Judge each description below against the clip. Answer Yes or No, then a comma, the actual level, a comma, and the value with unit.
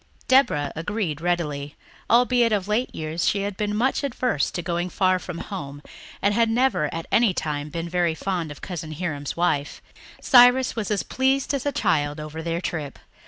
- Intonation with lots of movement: Yes, wide, 6.4 semitones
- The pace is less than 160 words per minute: No, average, 180 wpm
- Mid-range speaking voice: Yes, medium, 180 Hz